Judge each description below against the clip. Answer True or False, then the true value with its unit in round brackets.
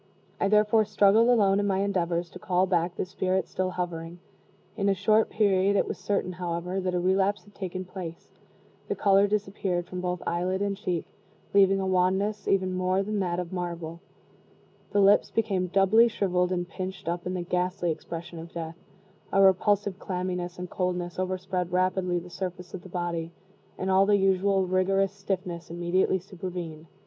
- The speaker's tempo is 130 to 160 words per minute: False (175 wpm)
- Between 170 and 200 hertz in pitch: True (185 Hz)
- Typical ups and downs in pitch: False (1.8 semitones)